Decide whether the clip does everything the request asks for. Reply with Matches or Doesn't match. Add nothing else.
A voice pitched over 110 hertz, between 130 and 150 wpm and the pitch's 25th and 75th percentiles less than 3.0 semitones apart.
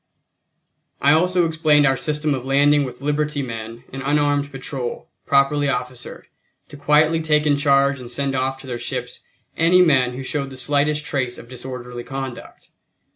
Doesn't match